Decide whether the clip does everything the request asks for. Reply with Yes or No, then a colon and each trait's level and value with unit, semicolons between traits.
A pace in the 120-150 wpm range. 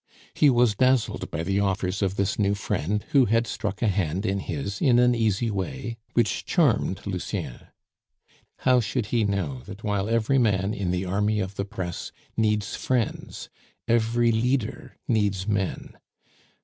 No: average, 160 wpm